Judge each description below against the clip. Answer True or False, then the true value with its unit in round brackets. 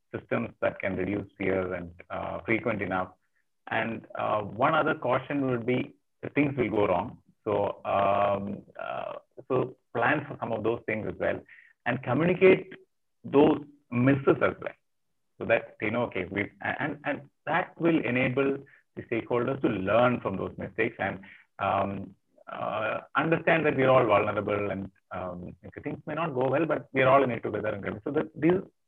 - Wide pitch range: True (6.5 semitones)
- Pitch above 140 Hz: False (120 Hz)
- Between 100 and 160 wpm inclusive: False (170 wpm)